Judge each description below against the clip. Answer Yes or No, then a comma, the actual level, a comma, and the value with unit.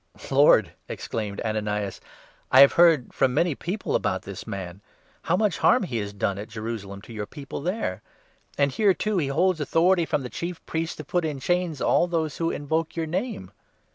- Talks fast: Yes, fast, 210 wpm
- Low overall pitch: No, medium, 145 Hz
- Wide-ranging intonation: Yes, wide, 8.1 semitones